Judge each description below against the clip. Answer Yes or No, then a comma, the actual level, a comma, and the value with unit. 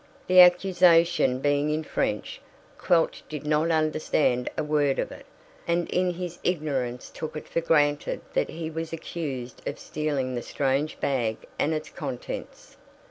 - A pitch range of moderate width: Yes, average, 3.4 semitones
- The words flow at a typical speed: Yes, average, 150 wpm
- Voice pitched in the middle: Yes, medium, 155 Hz